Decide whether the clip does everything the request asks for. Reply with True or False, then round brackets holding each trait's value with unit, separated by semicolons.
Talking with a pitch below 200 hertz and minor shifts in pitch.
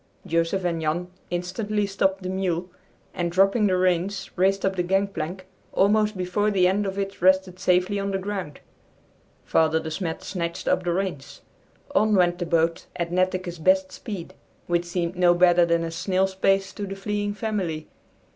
True (185 Hz; 2.0 semitones)